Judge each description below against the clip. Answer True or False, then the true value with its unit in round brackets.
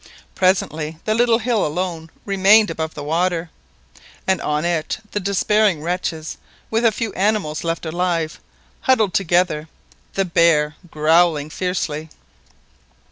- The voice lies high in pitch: False (175 Hz)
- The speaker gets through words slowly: True (120 wpm)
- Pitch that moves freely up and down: False (3.8 semitones)